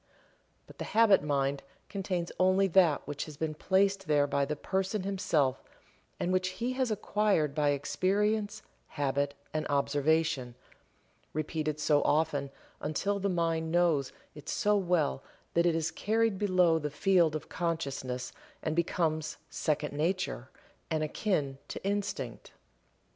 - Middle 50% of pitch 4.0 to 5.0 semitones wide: Yes, average, 4.6 semitones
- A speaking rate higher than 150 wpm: No, slow, 135 wpm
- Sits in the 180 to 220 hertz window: No, medium, 160 Hz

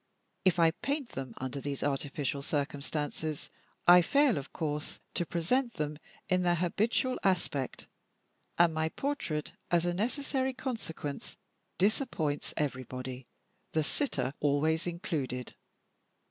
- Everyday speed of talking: No, slow, 120 wpm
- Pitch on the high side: No, medium, 160 Hz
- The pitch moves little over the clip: No, average, 4.8 semitones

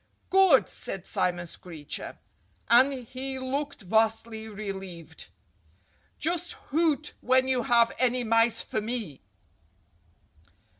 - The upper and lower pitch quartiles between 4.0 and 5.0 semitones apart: Yes, average, 4.3 semitones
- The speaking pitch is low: No, high, 235 Hz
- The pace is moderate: No, slow, 100 wpm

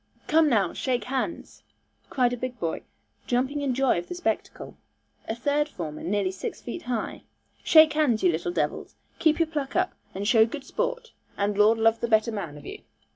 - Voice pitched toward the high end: Yes, high, 240 Hz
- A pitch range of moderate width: No, wide, 6.2 semitones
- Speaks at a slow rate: No, average, 190 wpm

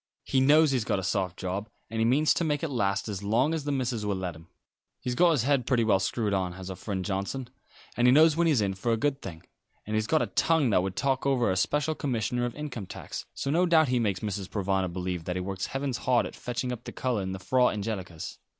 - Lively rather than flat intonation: Yes, wide, 5.9 semitones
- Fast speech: Yes, fast, 260 wpm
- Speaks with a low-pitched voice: Yes, low, 115 Hz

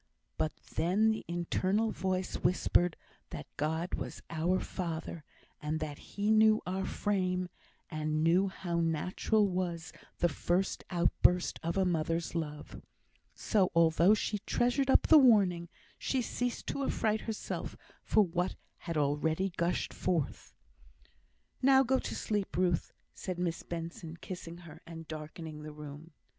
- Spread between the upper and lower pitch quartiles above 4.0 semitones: No, average, 3.3 semitones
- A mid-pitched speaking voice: Yes, medium, 175 Hz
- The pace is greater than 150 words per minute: No, average, 140 wpm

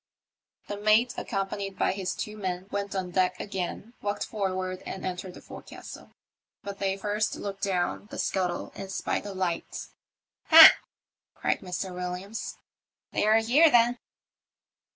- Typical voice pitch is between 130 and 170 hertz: No, high, 195 Hz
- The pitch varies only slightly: Yes, narrow, 2.1 semitones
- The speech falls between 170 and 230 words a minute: No, average, 150 wpm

